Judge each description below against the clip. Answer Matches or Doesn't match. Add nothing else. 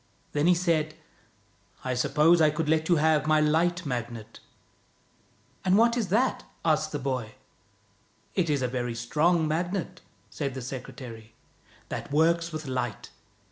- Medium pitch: Matches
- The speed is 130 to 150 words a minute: Doesn't match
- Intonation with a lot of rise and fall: Doesn't match